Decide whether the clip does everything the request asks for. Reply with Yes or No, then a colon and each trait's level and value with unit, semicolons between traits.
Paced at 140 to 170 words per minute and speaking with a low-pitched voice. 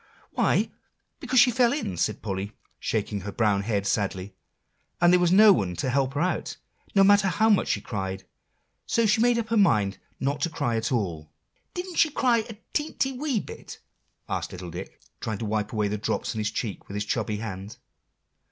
No: average, 200 wpm; low, 115 Hz